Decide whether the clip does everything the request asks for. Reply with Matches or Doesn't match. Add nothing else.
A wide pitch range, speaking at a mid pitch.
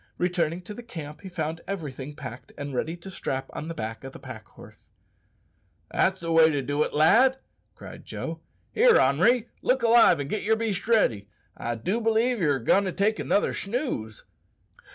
Matches